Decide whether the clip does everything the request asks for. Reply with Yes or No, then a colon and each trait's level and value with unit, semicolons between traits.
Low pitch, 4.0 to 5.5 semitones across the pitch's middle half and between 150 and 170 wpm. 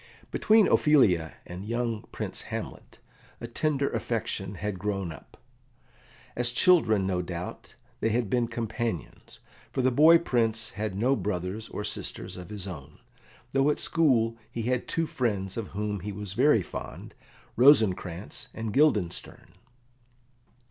No: low, 110 Hz; average, 4.4 semitones; average, 140 wpm